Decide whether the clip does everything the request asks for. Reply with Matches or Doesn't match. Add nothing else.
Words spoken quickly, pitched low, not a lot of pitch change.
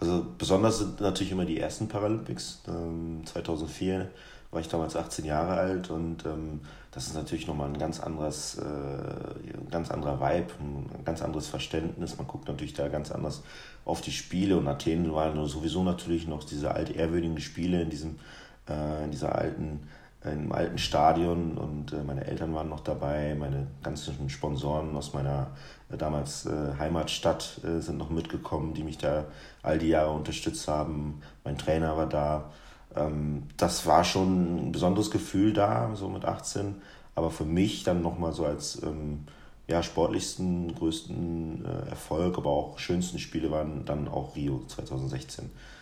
Doesn't match